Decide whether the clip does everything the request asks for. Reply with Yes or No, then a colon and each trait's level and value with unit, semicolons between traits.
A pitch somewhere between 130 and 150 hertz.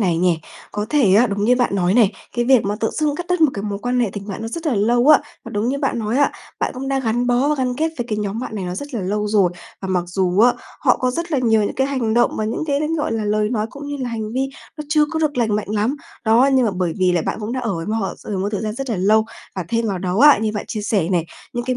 No: high, 225 Hz